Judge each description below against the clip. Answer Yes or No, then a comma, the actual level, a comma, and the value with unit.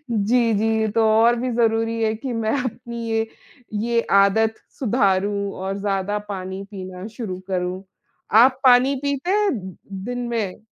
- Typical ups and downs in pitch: Yes, average, 3.1 semitones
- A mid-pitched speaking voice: No, high, 220 Hz